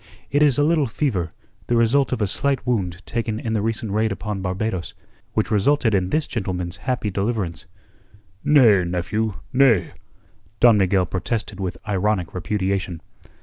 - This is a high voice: No, low, 105 Hz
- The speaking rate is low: No, average, 150 wpm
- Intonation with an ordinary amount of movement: Yes, average, 4.1 semitones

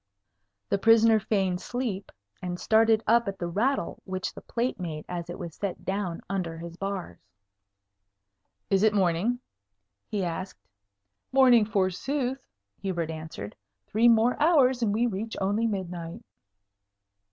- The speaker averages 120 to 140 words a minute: Yes, slow, 135 wpm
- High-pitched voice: Yes, high, 200 Hz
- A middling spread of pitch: Yes, average, 4.4 semitones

